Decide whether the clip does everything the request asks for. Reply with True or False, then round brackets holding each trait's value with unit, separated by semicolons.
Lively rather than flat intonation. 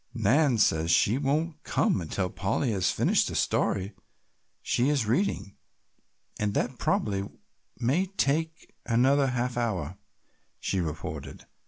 True (6.1 semitones)